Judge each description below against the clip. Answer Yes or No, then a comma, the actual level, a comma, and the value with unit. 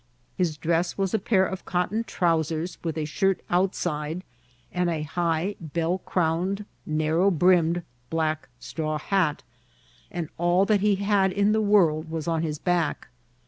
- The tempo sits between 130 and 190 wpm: Yes, average, 150 wpm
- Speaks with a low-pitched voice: No, medium, 175 Hz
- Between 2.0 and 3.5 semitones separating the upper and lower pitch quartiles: Yes, average, 3.1 semitones